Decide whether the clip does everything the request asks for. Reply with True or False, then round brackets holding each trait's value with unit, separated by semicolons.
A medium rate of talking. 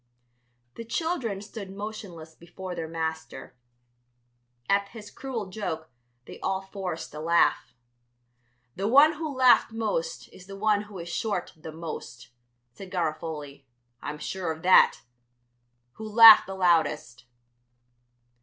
False (125 wpm)